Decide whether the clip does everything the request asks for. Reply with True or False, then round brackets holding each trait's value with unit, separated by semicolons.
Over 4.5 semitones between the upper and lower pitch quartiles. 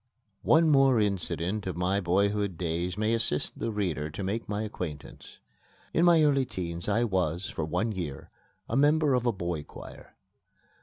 True (5.0 semitones)